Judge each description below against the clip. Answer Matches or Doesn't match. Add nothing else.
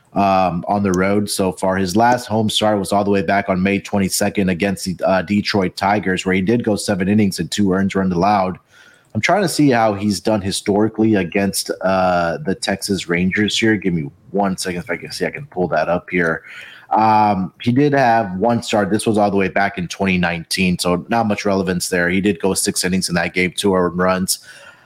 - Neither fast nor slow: Doesn't match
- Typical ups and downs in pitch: Doesn't match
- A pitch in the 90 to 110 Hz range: Matches